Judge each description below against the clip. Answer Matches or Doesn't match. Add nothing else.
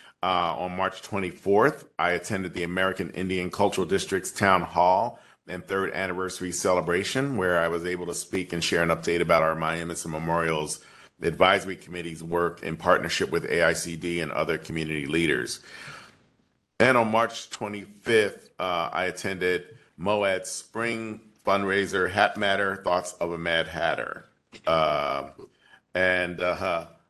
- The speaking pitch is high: Doesn't match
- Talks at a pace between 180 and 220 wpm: Doesn't match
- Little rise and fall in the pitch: Matches